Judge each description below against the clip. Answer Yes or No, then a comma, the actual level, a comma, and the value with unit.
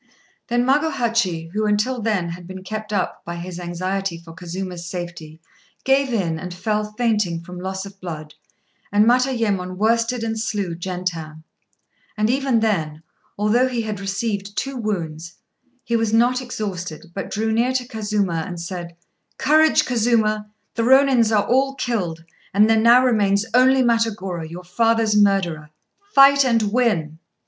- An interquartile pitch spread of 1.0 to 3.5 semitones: No, average, 4.7 semitones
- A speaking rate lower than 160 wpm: Yes, average, 150 wpm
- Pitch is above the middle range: Yes, high, 210 Hz